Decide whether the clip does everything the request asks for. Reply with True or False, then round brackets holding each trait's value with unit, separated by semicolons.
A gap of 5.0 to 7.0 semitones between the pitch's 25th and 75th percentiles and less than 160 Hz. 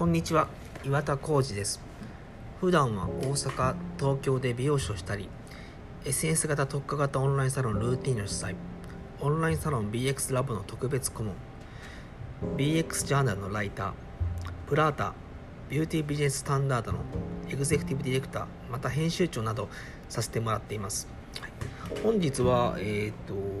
True (5.6 semitones; 135 Hz)